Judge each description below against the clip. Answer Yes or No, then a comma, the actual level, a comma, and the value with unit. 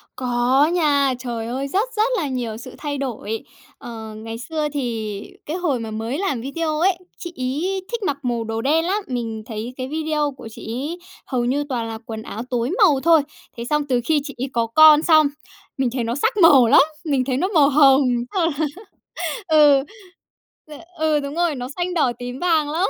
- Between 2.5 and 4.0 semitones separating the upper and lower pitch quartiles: No, average, 4.6 semitones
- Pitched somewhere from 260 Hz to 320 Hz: Yes, very high, 275 Hz